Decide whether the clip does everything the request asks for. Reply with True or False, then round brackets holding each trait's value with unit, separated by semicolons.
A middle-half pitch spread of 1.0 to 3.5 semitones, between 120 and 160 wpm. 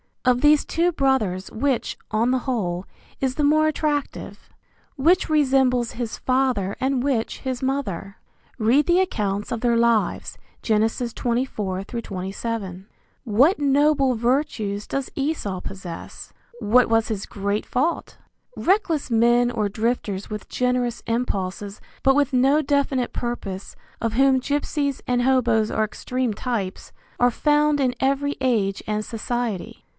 False (4.2 semitones; 135 wpm)